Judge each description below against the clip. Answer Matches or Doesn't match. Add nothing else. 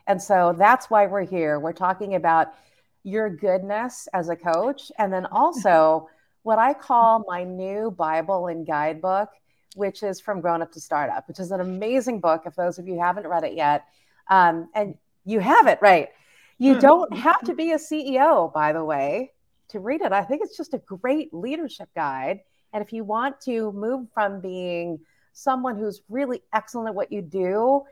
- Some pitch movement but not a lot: Doesn't match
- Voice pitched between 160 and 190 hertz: Doesn't match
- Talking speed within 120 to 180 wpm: Doesn't match